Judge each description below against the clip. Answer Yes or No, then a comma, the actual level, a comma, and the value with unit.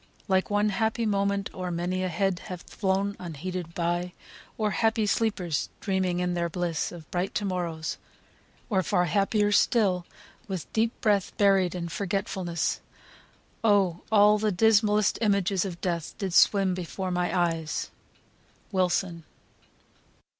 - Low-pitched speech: No, medium, 185 Hz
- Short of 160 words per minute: Yes, slow, 135 wpm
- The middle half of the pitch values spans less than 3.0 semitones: Yes, narrow, 2.6 semitones